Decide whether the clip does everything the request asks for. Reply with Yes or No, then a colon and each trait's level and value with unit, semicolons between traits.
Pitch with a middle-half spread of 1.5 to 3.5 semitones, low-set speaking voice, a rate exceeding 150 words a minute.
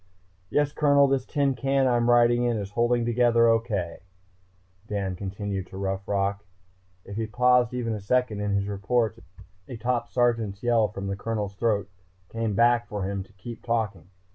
Yes: average, 3.2 semitones; low, 115 Hz; average, 165 wpm